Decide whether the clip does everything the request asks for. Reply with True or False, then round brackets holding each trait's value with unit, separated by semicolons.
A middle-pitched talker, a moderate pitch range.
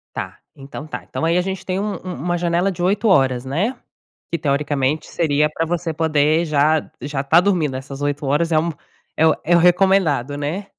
True (160 Hz; 3.5 semitones)